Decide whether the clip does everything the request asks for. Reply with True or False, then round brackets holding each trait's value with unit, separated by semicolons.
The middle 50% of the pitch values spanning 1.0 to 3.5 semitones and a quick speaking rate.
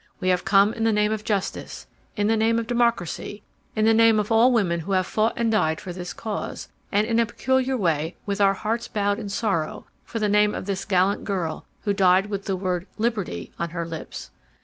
True (3.2 semitones; 220 wpm)